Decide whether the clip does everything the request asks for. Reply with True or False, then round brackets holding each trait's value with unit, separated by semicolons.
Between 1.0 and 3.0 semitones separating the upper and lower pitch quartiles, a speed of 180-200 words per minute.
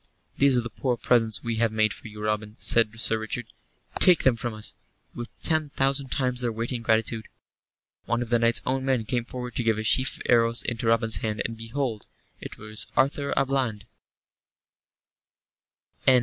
True (2.4 semitones; 190 wpm)